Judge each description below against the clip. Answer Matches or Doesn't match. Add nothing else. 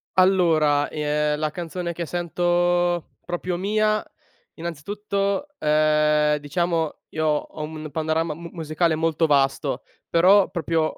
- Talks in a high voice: Doesn't match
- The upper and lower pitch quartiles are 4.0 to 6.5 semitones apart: Doesn't match